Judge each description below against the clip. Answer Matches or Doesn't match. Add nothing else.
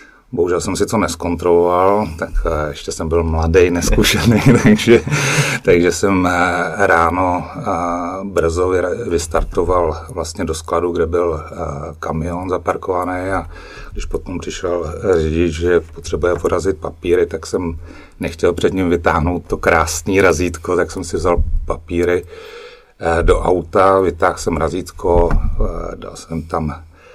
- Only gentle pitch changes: Matches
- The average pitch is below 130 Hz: Matches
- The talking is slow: Doesn't match